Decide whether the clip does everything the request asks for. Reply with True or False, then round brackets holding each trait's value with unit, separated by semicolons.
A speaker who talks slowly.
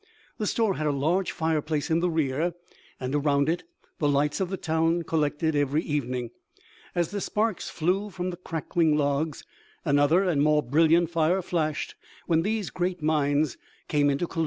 False (175 wpm)